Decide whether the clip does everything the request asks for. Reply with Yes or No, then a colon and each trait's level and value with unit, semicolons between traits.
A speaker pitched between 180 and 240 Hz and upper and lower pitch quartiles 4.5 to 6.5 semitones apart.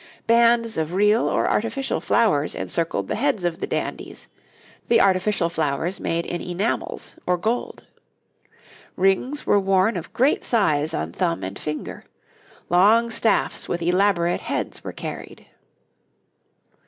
Yes: high, 190 Hz; average, 5.0 semitones